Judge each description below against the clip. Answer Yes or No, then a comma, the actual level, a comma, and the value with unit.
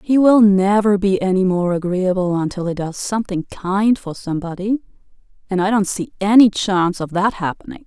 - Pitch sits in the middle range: No, high, 195 Hz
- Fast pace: No, average, 175 wpm